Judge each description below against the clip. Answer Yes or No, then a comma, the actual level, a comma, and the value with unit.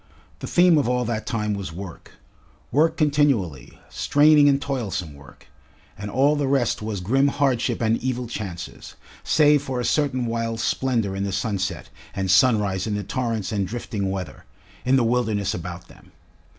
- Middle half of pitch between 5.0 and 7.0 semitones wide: Yes, wide, 5.4 semitones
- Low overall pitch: Yes, low, 115 Hz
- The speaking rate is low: No, average, 165 wpm